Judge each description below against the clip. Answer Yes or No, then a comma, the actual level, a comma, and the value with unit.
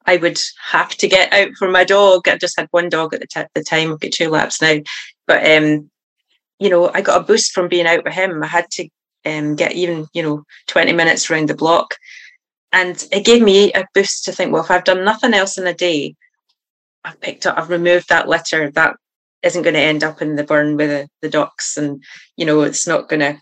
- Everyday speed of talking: No, fast, 240 wpm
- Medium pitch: Yes, medium, 175 Hz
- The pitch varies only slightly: No, average, 3.2 semitones